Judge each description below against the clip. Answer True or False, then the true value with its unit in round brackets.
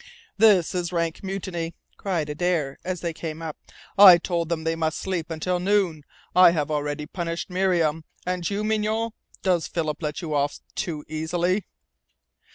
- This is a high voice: False (170 Hz)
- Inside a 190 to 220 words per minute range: False (160 wpm)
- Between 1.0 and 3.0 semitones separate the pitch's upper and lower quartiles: True (2.7 semitones)